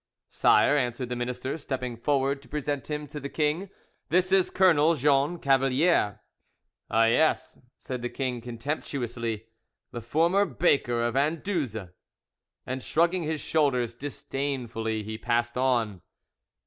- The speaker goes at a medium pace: No, slow, 130 wpm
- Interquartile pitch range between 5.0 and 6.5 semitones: No, average, 4.1 semitones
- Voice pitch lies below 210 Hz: Yes, low, 135 Hz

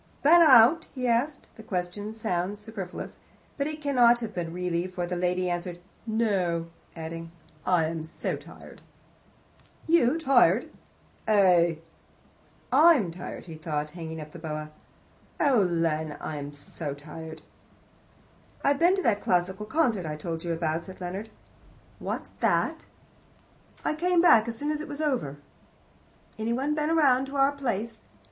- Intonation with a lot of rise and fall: Yes, wide, 7.8 semitones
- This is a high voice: Yes, high, 195 Hz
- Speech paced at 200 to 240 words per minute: No, average, 155 wpm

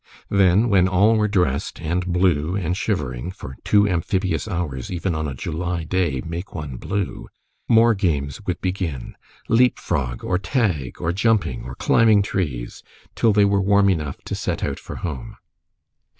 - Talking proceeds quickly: No, average, 165 wpm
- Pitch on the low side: Yes, very low, 90 Hz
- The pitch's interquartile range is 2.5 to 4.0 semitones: No, average, 4.7 semitones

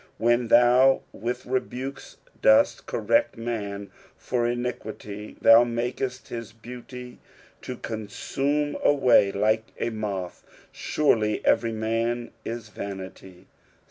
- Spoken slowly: Yes, slow, 110 wpm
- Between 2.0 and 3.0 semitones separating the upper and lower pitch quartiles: Yes, narrow, 2.6 semitones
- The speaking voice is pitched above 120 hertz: No, low, 115 Hz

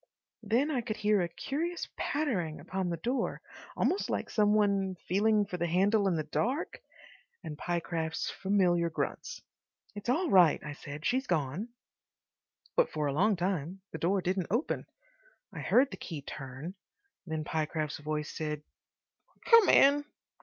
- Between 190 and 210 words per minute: No, average, 155 wpm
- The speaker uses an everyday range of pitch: No, wide, 5.7 semitones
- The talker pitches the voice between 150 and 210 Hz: Yes, medium, 185 Hz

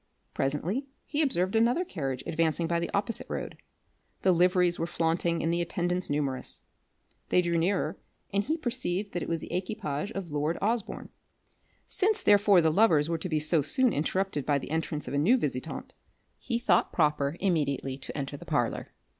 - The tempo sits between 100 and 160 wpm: No, average, 180 wpm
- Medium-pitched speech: Yes, medium, 170 Hz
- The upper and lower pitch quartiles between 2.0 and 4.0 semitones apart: No, average, 4.8 semitones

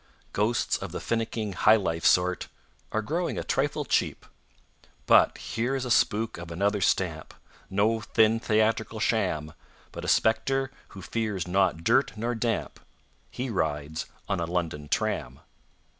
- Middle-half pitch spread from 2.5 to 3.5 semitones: No, average, 4.4 semitones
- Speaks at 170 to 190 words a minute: No, average, 145 wpm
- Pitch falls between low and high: No, low, 105 Hz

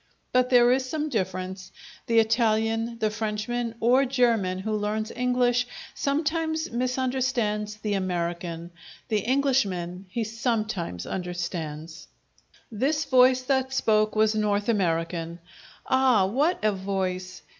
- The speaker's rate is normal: No, slow, 115 wpm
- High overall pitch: Yes, high, 220 Hz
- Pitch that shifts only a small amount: No, average, 5.0 semitones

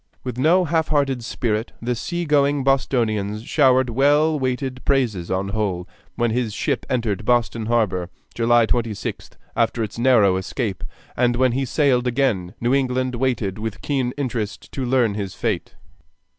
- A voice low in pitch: Yes, low, 120 Hz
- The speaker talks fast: No, average, 150 wpm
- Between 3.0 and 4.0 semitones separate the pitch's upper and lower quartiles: Yes, average, 3.4 semitones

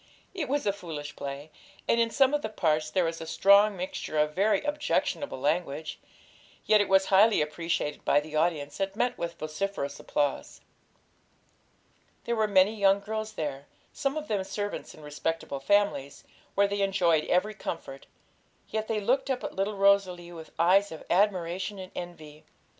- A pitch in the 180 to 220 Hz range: Yes, high, 190 Hz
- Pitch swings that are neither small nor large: Yes, average, 5.0 semitones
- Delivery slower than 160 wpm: No, average, 170 wpm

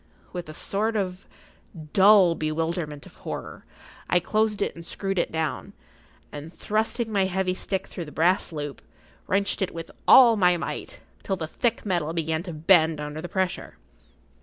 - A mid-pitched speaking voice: Yes, medium, 180 Hz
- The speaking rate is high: No, average, 170 wpm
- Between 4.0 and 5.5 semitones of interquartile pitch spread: No, average, 3.5 semitones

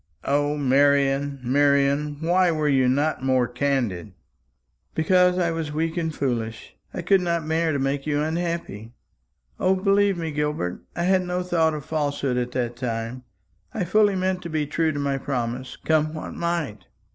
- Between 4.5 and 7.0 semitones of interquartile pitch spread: No, average, 4.0 semitones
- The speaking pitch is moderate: Yes, medium, 150 Hz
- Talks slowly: No, average, 170 wpm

